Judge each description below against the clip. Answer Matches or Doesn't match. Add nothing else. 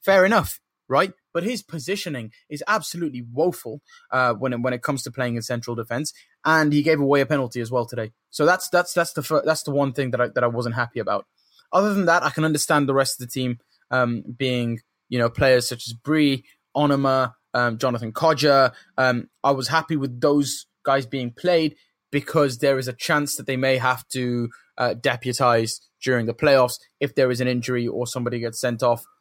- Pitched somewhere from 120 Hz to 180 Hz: Matches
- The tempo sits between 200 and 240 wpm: Matches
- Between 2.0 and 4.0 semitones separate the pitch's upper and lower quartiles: Matches